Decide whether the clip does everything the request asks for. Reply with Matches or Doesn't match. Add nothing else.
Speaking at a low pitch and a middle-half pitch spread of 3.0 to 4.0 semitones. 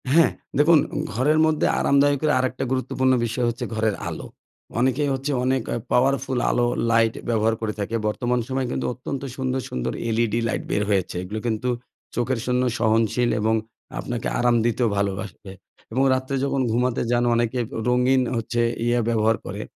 Doesn't match